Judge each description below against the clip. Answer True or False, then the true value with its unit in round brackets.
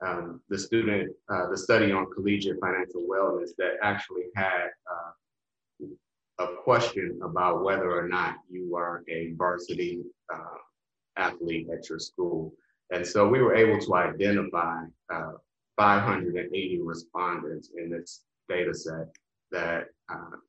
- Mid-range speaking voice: False (90 Hz)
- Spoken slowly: True (125 wpm)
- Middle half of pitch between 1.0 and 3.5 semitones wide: True (2.9 semitones)